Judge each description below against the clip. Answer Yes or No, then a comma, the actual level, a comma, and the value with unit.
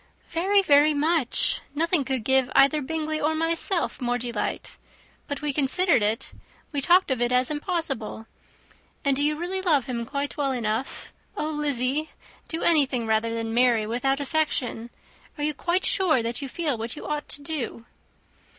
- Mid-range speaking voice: No, very high, 285 Hz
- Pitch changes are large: No, average, 4.2 semitones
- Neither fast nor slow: Yes, average, 170 wpm